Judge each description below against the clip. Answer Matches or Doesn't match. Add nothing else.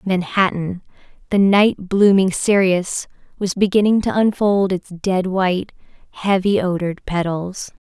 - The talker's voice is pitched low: Doesn't match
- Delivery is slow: Matches